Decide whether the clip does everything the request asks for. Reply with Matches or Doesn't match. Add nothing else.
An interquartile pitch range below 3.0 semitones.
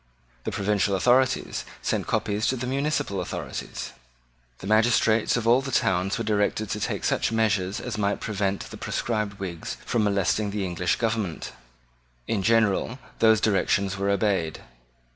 Matches